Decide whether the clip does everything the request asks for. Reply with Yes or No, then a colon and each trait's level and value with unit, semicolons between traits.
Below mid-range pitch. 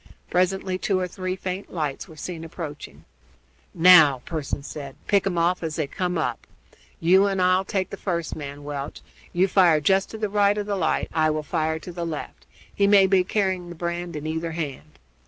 No: medium, 175 Hz